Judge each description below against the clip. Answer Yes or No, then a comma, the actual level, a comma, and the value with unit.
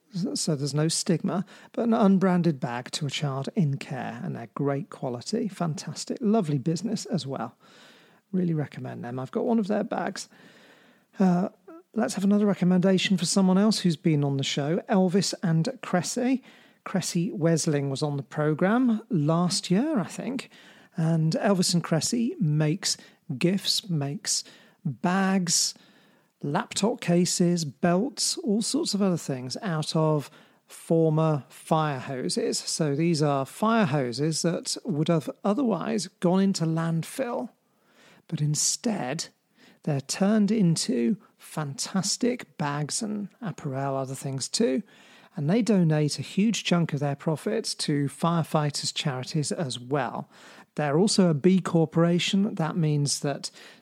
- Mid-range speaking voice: Yes, medium, 180 Hz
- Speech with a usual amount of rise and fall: No, wide, 5.7 semitones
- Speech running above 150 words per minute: No, average, 140 wpm